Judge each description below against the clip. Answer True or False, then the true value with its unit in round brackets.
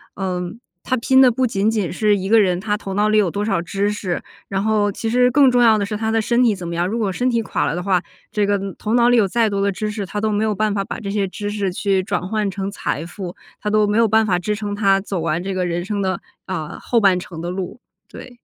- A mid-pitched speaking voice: False (205 Hz)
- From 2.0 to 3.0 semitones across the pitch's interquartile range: True (2.6 semitones)